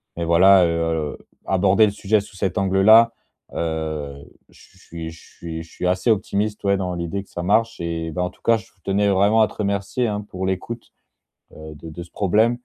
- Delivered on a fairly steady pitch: No, average, 3.6 semitones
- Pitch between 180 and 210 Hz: No, very low, 95 Hz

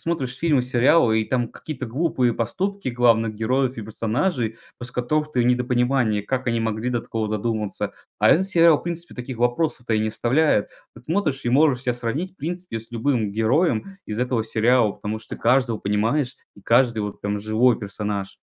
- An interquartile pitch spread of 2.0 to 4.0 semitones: Yes, average, 3.6 semitones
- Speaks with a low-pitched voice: Yes, low, 120 Hz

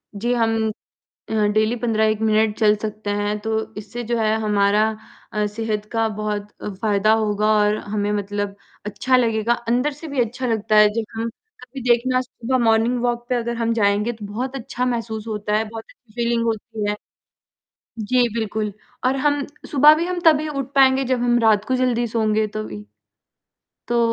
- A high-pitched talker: Yes, high, 225 Hz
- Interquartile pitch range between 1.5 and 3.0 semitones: Yes, narrow, 2.4 semitones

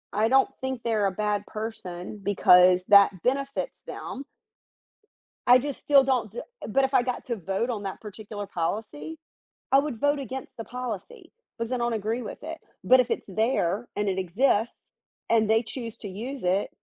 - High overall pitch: Yes, high, 225 Hz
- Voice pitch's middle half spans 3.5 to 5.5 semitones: Yes, average, 4.2 semitones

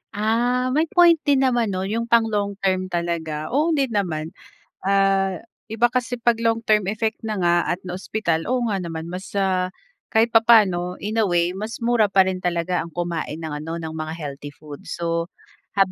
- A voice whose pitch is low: No, high, 195 Hz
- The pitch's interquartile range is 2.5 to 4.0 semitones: No, average, 5.0 semitones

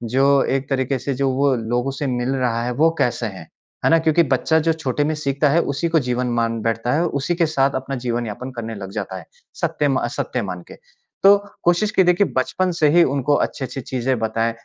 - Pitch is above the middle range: No, low, 135 Hz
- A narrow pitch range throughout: No, average, 4.2 semitones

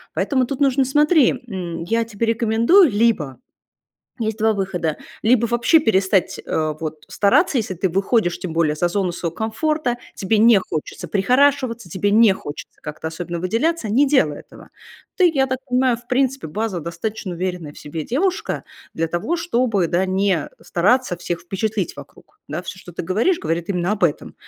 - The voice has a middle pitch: No, high, 205 Hz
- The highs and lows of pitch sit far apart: Yes, wide, 6.2 semitones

